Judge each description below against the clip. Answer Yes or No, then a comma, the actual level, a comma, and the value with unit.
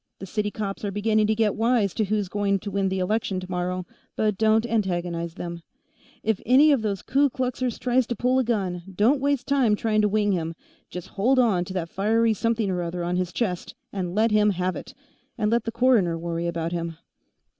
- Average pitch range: Yes, average, 4.0 semitones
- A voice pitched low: No, high, 210 Hz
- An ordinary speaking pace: No, fast, 215 wpm